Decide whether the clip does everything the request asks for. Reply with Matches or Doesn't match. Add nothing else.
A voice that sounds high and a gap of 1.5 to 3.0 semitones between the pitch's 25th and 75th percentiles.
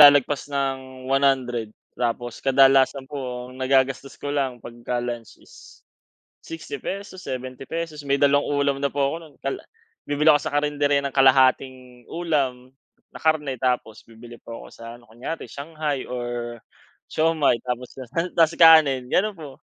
Doesn't match